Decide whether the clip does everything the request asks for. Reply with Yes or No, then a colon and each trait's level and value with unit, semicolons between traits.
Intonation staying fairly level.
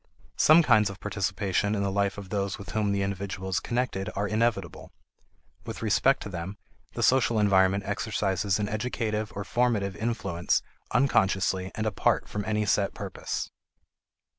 Yes: narrow, 2.0 semitones